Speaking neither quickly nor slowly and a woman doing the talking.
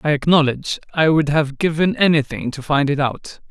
No: average, 190 wpm; male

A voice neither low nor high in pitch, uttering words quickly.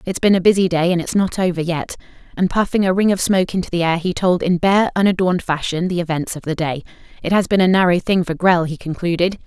Yes: medium, 180 Hz; fast, 255 wpm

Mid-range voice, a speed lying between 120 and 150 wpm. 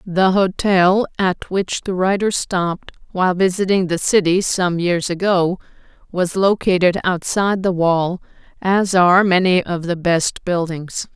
Yes: medium, 180 Hz; average, 140 wpm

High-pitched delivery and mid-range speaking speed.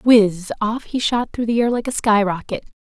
No: high, 220 Hz; fast, 225 wpm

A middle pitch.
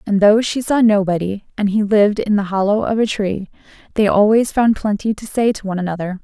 No: high, 205 Hz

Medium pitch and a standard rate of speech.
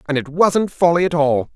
No: medium, 160 Hz; fast, 230 wpm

